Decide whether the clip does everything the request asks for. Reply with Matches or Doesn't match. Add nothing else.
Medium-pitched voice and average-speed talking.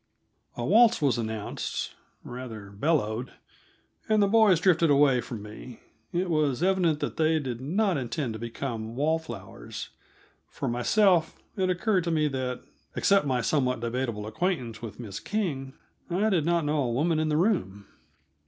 Matches